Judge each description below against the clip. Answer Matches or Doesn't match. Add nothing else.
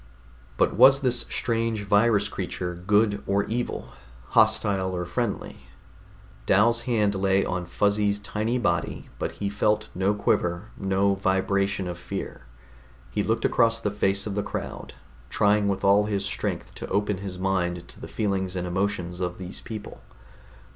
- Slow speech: Doesn't match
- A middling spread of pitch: Doesn't match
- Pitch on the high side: Doesn't match